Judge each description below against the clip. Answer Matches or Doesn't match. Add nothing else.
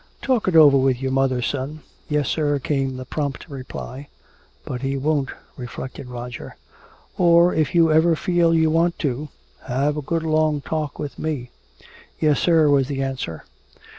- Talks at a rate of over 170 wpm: Doesn't match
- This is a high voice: Doesn't match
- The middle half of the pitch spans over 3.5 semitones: Doesn't match